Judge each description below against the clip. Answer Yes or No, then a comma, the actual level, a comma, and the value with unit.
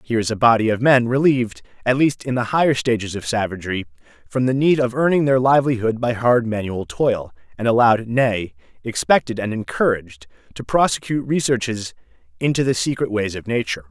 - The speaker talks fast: No, average, 175 wpm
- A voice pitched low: Yes, low, 115 Hz